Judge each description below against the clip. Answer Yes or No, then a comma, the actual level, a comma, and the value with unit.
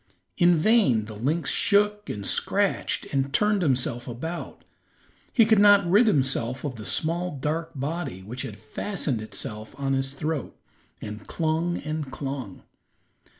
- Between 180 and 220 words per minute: No, average, 145 wpm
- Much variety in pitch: Yes, wide, 6.1 semitones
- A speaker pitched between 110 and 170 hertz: Yes, medium, 140 Hz